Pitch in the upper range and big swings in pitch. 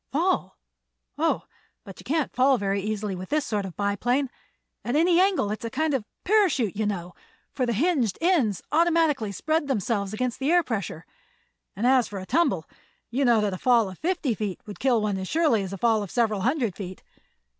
Yes: high, 235 Hz; wide, 6.2 semitones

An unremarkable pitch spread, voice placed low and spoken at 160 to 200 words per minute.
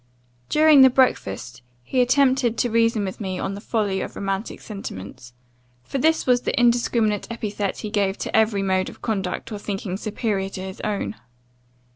No: average, 3.8 semitones; high, 210 Hz; average, 170 wpm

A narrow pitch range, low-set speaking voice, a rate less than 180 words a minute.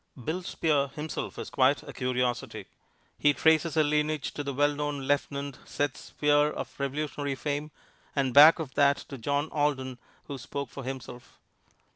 No: narrow, 1.7 semitones; medium, 145 Hz; average, 160 wpm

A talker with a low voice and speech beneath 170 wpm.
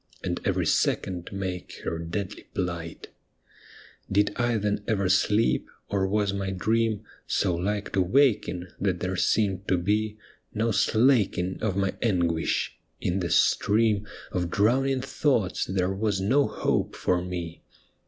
Yes: low, 100 Hz; average, 140 wpm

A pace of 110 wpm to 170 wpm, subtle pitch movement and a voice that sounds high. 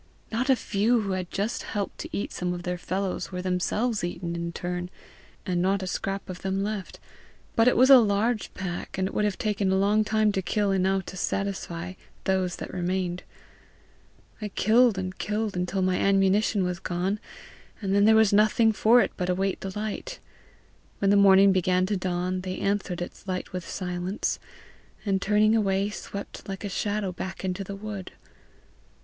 No: average, 185 wpm; narrow, 2.3 semitones; high, 195 Hz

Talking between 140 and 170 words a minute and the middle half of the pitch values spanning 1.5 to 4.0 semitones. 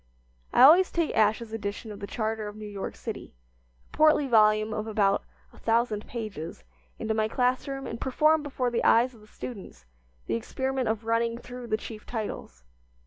No: average, 185 wpm; average, 2.8 semitones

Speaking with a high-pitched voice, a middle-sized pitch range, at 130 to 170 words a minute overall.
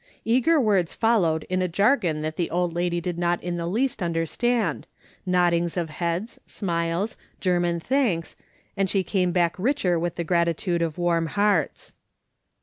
No: medium, 175 Hz; average, 3.0 semitones; average, 155 wpm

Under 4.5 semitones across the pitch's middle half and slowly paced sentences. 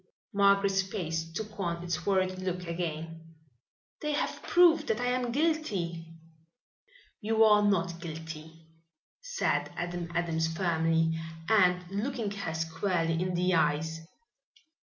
Yes: average, 3.9 semitones; slow, 120 wpm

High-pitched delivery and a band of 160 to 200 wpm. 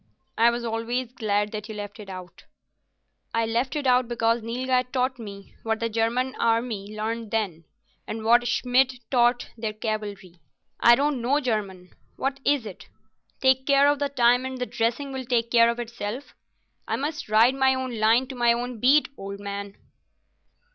Yes: high, 235 Hz; average, 175 wpm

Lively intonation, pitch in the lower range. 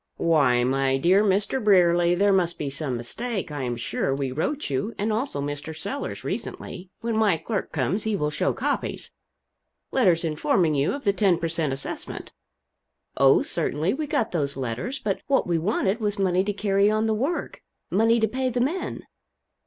No: wide, 6.6 semitones; medium, 185 Hz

